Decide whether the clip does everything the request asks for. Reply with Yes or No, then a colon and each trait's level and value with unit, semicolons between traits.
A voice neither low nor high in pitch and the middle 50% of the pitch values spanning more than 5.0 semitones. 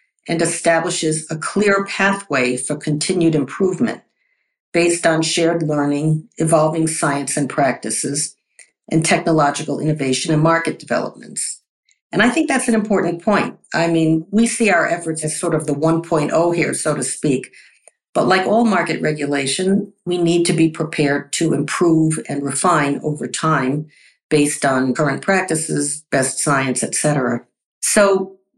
No: medium, 160 Hz; average, 3.3 semitones